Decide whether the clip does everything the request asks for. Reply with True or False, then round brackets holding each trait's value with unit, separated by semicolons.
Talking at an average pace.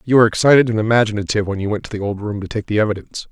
False (290 wpm)